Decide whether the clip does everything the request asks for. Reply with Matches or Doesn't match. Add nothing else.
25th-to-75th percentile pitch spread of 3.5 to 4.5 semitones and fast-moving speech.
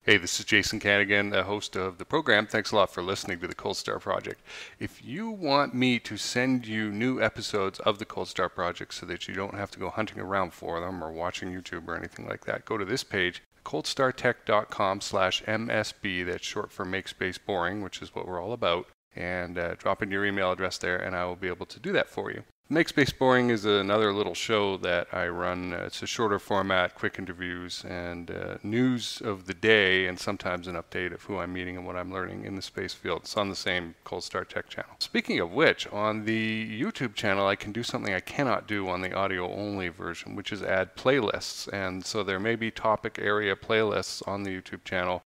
Doesn't match